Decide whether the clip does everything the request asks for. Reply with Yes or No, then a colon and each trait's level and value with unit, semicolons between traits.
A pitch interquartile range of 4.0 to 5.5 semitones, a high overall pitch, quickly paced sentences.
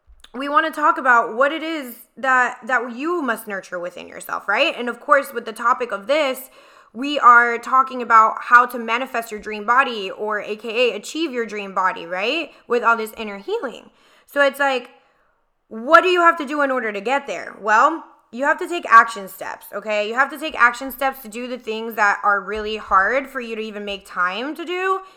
Yes: average, 4.4 semitones; high, 245 Hz; fast, 215 wpm